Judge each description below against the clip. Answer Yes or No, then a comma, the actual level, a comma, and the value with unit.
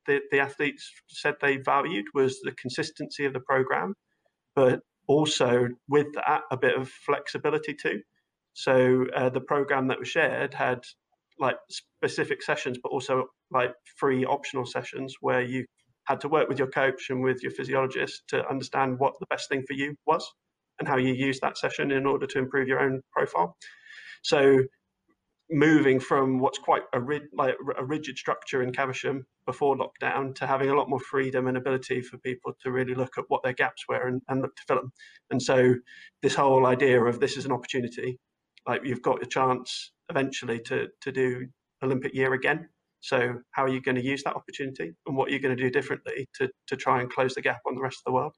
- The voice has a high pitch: No, low, 135 Hz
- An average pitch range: No, narrow, 1.9 semitones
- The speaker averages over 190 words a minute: Yes, average, 200 wpm